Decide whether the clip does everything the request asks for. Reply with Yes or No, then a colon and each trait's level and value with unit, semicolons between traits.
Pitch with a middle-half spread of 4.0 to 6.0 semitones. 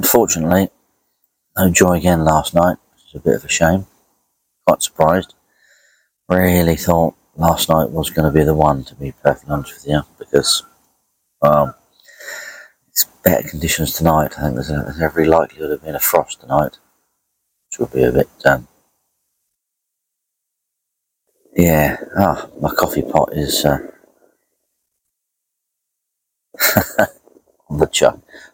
No: average, 2.7 semitones